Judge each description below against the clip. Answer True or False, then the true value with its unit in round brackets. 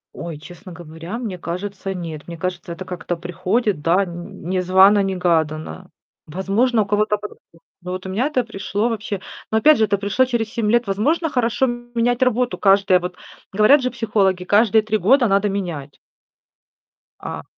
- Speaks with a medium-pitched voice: False (200 Hz)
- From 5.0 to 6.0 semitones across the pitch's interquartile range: False (4.1 semitones)